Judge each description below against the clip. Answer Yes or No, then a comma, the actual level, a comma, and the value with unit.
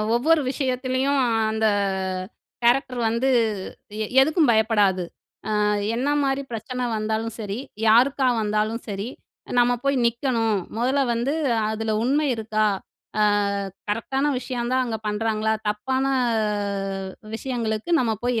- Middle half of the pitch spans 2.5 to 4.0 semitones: Yes, average, 3.3 semitones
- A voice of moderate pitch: No, high, 235 Hz